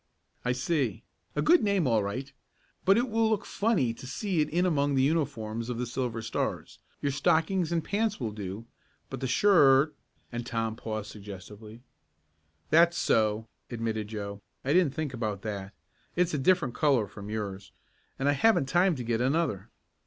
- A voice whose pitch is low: Yes, low, 130 Hz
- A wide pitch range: Yes, wide, 7.0 semitones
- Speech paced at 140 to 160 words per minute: No, average, 175 wpm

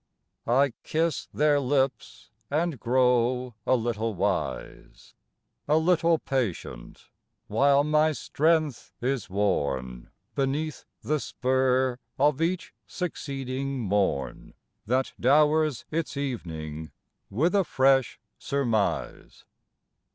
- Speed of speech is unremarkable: No, slow, 95 wpm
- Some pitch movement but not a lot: Yes, average, 4.6 semitones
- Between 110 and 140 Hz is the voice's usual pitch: Yes, low, 135 Hz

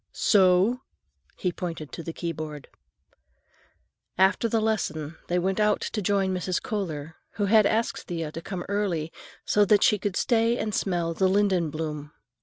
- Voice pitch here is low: No, medium, 185 Hz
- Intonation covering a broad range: No, average, 3.9 semitones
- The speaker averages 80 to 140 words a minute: No, average, 160 wpm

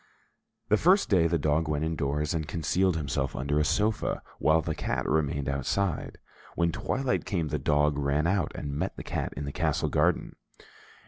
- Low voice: Yes, very low, 80 Hz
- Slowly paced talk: No, average, 180 wpm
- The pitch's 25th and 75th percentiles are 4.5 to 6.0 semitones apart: No, average, 2.9 semitones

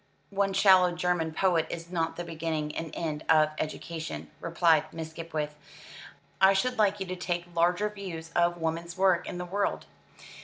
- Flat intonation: Yes, narrow, 2.3 semitones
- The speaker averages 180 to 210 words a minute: No, average, 165 wpm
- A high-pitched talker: No, medium, 170 Hz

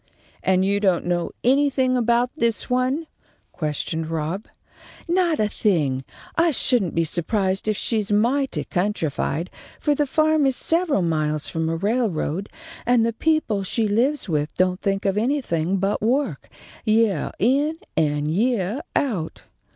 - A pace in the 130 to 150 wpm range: Yes, average, 145 wpm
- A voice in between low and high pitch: No, high, 210 Hz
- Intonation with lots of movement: Yes, wide, 6.7 semitones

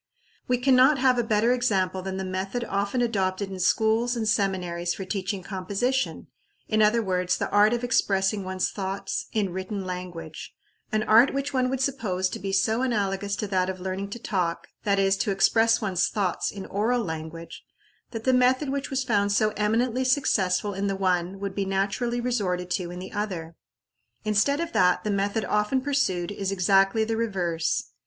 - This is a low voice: No, high, 200 Hz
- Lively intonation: No, average, 3.8 semitones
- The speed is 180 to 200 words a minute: Yes, average, 185 wpm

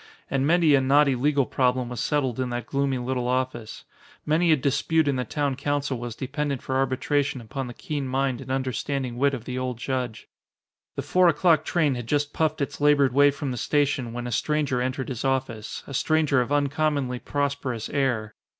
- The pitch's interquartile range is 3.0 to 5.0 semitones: No, narrow, 2.5 semitones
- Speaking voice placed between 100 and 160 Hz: Yes, low, 135 Hz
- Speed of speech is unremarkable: Yes, average, 195 wpm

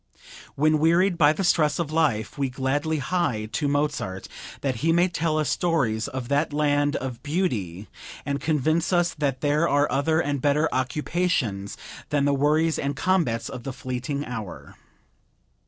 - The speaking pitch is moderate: Yes, medium, 145 Hz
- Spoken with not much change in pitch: No, average, 3.5 semitones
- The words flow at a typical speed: Yes, average, 160 wpm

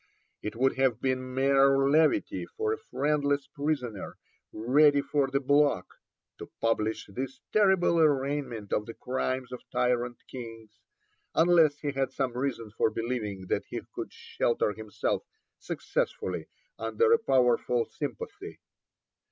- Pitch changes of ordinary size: Yes, average, 3.5 semitones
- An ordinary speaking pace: No, slow, 130 wpm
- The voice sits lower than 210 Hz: Yes, low, 135 Hz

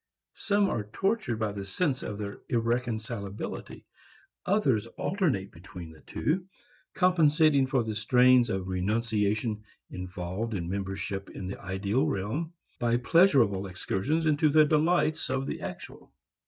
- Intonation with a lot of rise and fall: Yes, wide, 7.4 semitones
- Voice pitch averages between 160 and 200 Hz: No, low, 115 Hz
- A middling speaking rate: No, slow, 130 wpm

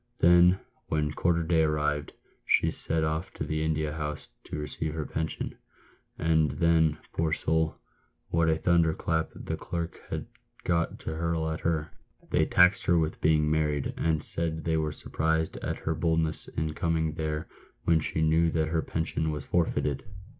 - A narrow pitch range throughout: Yes, narrow, 1.1 semitones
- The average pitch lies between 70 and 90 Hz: Yes, very low, 80 Hz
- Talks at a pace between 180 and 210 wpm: No, average, 165 wpm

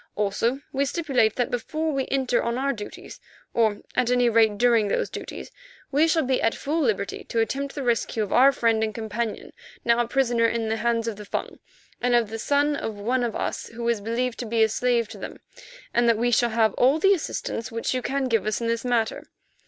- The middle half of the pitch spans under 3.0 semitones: Yes, narrow, 2.5 semitones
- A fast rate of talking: Yes, fast, 225 wpm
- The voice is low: No, high, 235 Hz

